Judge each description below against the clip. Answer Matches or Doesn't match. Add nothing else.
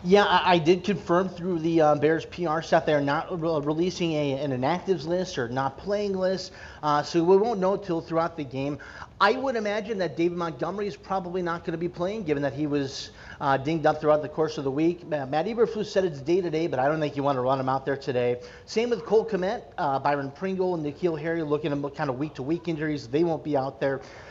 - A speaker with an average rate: Doesn't match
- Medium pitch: Matches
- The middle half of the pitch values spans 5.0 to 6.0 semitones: Doesn't match